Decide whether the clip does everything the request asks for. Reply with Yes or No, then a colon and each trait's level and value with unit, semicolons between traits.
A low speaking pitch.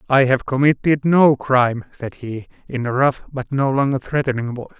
Yes: low, 130 Hz